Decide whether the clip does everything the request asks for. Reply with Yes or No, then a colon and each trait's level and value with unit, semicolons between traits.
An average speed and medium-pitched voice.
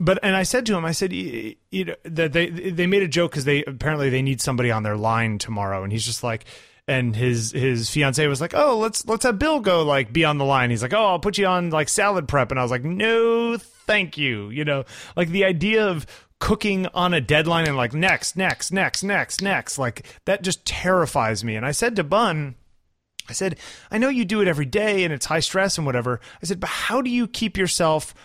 No: fast, 240 wpm; medium, 165 Hz